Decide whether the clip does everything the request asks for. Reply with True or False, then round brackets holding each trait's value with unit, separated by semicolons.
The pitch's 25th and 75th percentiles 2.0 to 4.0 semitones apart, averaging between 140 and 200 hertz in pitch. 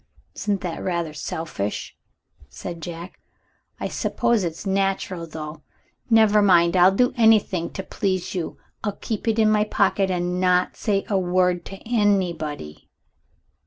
True (3.3 semitones; 185 Hz)